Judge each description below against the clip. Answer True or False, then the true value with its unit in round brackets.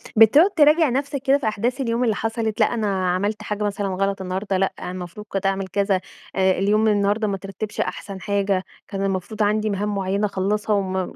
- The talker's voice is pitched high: True (205 Hz)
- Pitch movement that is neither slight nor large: False (2.1 semitones)